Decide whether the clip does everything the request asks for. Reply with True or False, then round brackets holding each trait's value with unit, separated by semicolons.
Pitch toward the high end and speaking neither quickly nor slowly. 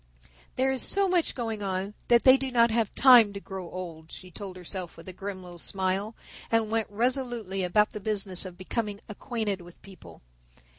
True (205 Hz; 190 wpm)